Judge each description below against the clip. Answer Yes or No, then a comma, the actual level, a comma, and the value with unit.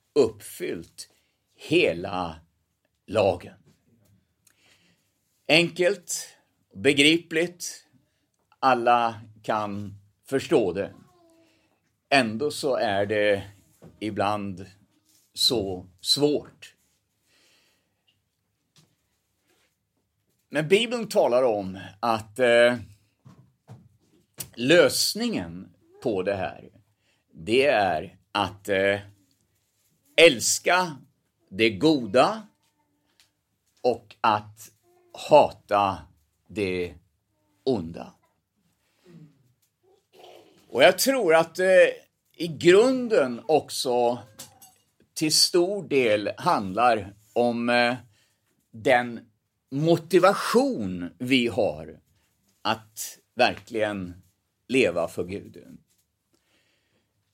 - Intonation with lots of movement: Yes, wide, 7.0 semitones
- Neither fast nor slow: No, slow, 65 wpm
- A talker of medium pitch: No, low, 110 Hz